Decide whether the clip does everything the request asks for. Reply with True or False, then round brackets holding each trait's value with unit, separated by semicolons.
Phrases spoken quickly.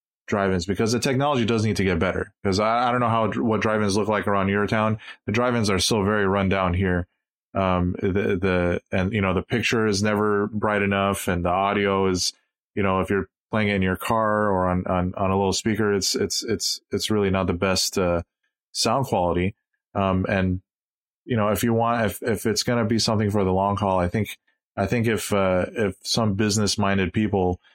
True (220 wpm)